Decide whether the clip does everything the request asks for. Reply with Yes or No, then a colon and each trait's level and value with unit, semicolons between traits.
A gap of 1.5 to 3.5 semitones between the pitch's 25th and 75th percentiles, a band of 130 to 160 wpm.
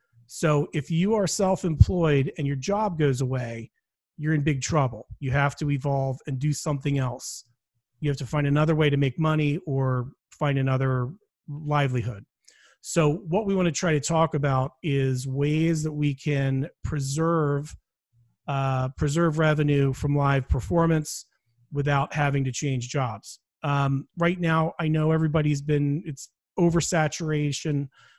Yes: average, 2.7 semitones; average, 150 wpm